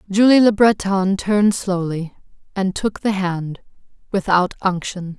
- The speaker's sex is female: Yes, female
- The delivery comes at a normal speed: No, slow, 115 wpm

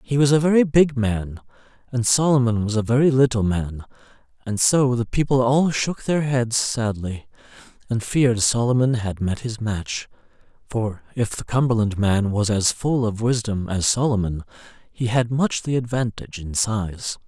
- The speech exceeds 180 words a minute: No, average, 165 wpm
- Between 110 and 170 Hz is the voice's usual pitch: Yes, low, 115 Hz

